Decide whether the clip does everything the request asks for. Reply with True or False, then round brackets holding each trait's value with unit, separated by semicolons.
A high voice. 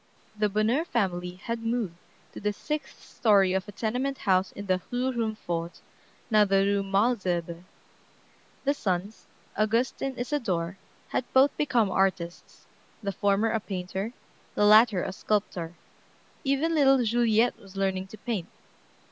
True (210 Hz)